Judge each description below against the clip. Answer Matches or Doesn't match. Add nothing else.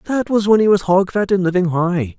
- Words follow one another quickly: Matches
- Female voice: Doesn't match